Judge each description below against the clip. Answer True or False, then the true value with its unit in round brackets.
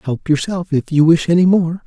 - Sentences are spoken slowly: False (225 wpm)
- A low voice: False (165 Hz)